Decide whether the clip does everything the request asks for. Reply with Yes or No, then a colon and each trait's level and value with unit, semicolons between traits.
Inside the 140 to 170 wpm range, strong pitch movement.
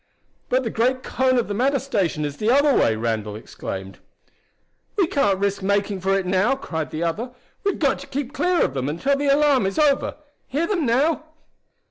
No: average, 195 wpm; wide, 7.4 semitones